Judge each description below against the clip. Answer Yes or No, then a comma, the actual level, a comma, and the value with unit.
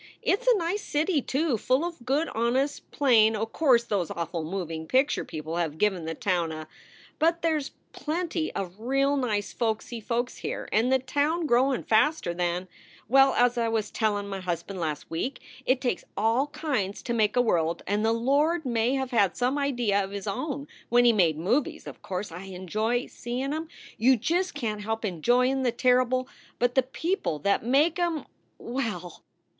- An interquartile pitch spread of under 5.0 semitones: No, wide, 5.5 semitones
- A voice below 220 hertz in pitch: No, high, 240 Hz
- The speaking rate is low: No, average, 185 wpm